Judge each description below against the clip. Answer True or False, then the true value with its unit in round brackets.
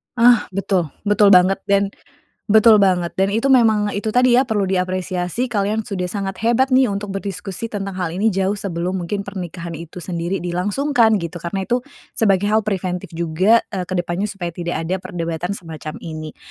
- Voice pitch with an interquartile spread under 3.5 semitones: True (3.1 semitones)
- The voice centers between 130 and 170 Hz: False (195 Hz)